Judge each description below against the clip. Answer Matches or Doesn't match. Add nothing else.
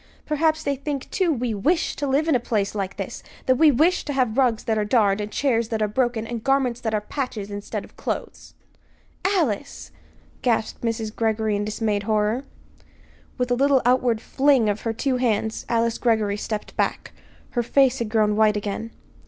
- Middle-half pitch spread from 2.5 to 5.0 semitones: Matches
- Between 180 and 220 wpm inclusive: Matches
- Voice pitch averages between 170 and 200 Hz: Doesn't match